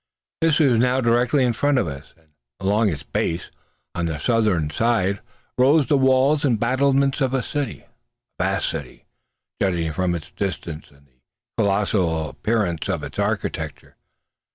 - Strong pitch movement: Yes, wide, 7.6 semitones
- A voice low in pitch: Yes, low, 105 Hz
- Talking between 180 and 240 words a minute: No, average, 155 wpm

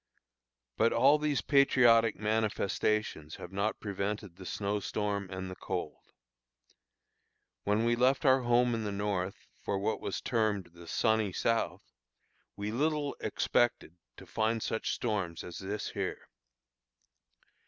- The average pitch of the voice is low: Yes, low, 110 Hz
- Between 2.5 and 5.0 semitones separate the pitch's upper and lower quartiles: Yes, average, 3.0 semitones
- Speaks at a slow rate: Yes, slow, 130 wpm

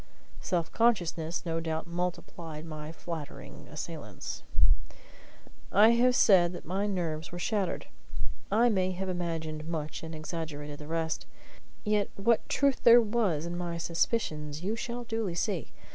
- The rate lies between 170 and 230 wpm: No, average, 140 wpm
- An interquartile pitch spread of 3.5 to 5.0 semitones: Yes, average, 4.3 semitones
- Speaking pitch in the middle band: Yes, medium, 175 Hz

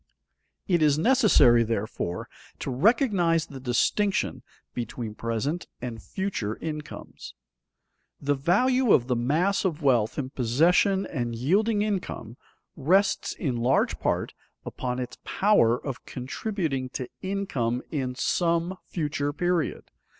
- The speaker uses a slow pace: Yes, slow, 120 wpm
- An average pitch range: No, wide, 7.3 semitones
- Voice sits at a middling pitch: Yes, medium, 145 Hz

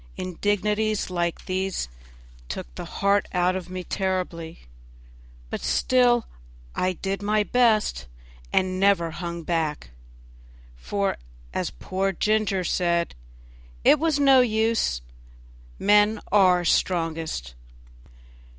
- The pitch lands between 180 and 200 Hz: Yes, high, 190 Hz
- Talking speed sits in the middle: No, slow, 105 wpm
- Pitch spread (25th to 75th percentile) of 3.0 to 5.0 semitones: Yes, average, 3.5 semitones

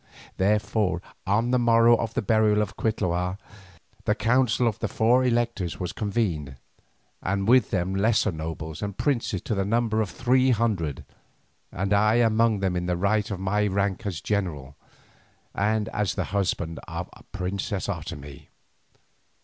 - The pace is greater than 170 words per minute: No, average, 150 wpm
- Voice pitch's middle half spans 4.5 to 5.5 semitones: No, average, 3.7 semitones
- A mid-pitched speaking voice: No, low, 100 Hz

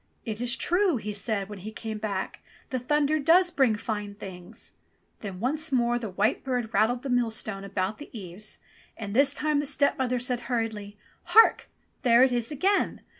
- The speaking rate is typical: Yes, average, 180 wpm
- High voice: Yes, high, 235 Hz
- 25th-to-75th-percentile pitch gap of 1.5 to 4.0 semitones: No, average, 4.4 semitones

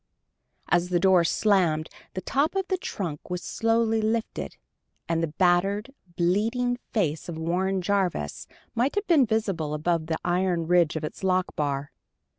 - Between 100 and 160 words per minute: Yes, average, 155 wpm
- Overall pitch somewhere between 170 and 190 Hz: Yes, medium, 185 Hz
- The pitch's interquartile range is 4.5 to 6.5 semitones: Yes, average, 4.9 semitones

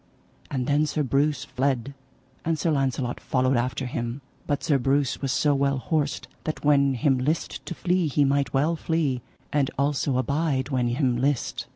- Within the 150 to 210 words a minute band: Yes, average, 175 wpm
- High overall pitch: No, medium, 140 Hz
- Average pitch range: No, narrow, 2.3 semitones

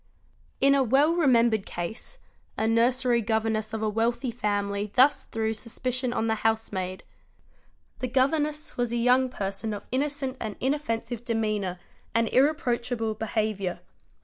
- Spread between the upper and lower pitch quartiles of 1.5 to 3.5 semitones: Yes, average, 3.0 semitones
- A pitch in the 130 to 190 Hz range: No, high, 230 Hz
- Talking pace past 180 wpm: No, average, 140 wpm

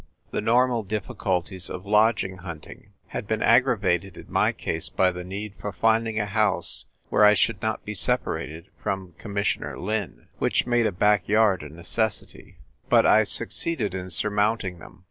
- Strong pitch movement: No, average, 3.0 semitones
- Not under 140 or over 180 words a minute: Yes, average, 165 wpm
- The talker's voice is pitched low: Yes, low, 105 Hz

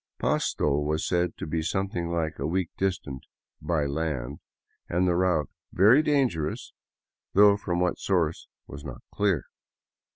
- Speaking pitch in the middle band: No, very low, 85 Hz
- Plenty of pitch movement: No, average, 3.8 semitones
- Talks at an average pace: Yes, average, 155 wpm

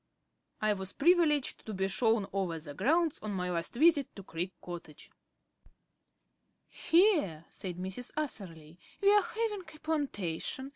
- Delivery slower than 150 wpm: Yes, average, 140 wpm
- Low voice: No, high, 215 Hz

